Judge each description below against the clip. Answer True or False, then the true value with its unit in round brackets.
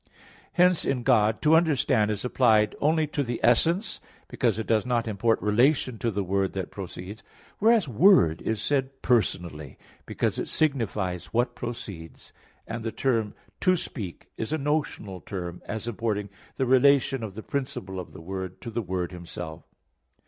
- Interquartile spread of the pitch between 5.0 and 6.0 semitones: True (5.6 semitones)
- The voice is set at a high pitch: False (115 Hz)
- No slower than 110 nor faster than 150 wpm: False (165 wpm)